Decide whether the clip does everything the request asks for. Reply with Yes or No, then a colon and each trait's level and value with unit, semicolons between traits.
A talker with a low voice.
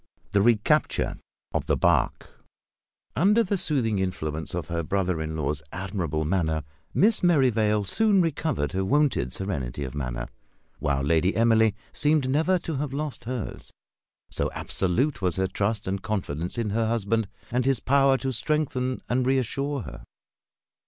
Yes: low, 110 Hz